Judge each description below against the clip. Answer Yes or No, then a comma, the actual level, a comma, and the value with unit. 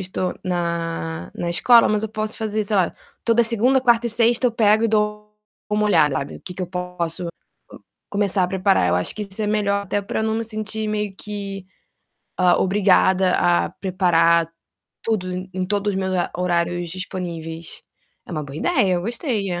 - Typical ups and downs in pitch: Yes, average, 3.4 semitones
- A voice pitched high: Yes, high, 195 Hz